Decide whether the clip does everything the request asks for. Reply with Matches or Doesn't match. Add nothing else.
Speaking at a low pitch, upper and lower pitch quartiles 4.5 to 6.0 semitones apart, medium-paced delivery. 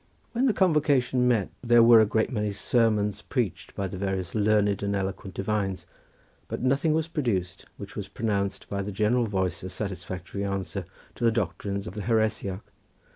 Doesn't match